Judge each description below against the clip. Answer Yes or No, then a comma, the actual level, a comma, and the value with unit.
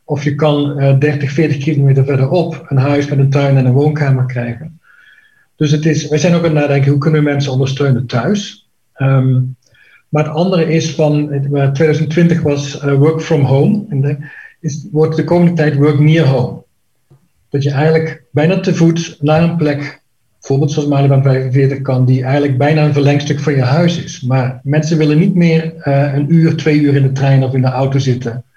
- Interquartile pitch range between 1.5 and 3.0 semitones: Yes, narrow, 2.5 semitones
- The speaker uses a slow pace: No, average, 195 wpm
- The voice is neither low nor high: Yes, medium, 145 Hz